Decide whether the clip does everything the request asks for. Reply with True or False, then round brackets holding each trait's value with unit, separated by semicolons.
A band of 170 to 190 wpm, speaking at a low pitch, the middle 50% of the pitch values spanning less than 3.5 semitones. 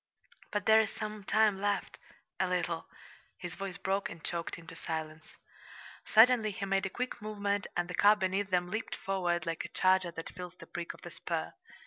False (185 wpm; 190 Hz; 2.9 semitones)